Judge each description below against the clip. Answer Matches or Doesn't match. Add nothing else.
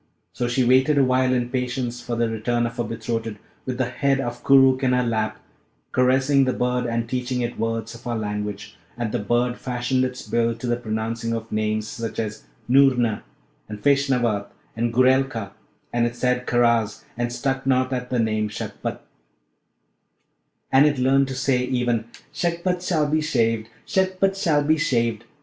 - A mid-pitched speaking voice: Doesn't match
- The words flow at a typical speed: Matches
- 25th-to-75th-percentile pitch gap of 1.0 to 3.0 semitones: Matches